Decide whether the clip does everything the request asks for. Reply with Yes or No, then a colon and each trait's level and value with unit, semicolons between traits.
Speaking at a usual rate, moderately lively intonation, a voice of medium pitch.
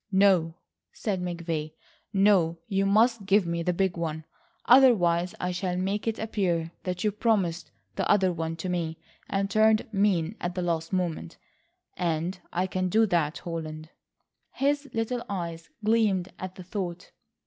Yes: average, 150 wpm; average, 3.3 semitones; medium, 180 Hz